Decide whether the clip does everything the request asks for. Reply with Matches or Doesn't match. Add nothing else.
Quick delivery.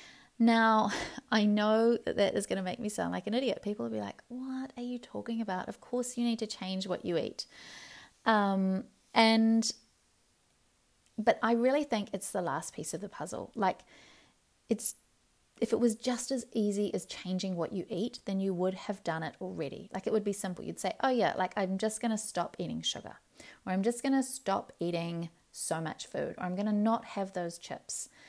Matches